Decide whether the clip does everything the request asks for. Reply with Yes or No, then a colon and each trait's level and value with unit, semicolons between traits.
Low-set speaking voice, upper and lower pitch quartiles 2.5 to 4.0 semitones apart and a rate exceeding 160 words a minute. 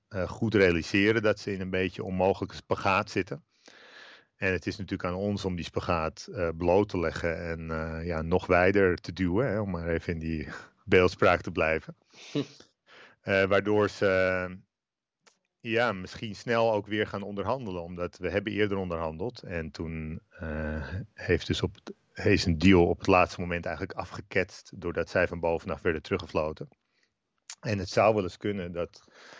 Yes: very low, 95 Hz; average, 3.0 semitones; average, 175 wpm